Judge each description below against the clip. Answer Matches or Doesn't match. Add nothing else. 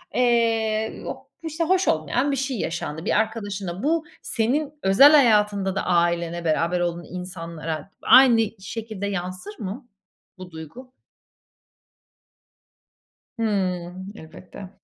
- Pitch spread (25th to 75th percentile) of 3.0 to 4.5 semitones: Doesn't match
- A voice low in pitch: Doesn't match